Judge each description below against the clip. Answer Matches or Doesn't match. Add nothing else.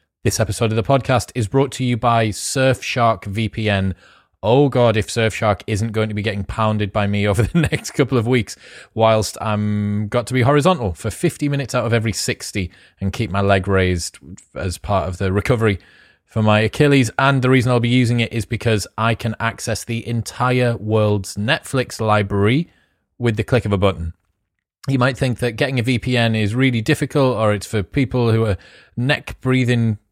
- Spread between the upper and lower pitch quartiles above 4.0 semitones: Doesn't match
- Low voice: Matches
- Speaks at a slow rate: Doesn't match